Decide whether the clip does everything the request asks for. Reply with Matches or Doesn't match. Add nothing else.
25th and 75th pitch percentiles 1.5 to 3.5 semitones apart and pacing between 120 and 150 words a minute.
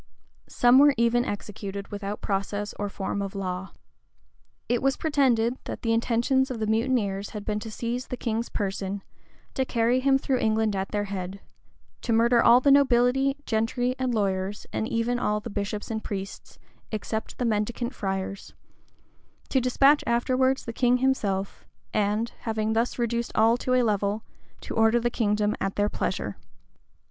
Doesn't match